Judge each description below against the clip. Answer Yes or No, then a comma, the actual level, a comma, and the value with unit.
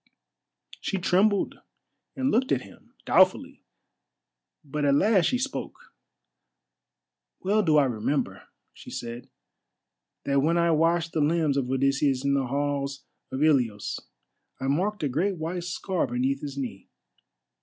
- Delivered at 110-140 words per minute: Yes, slow, 135 wpm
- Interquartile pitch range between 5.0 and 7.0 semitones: No, average, 4.5 semitones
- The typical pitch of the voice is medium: Yes, medium, 145 Hz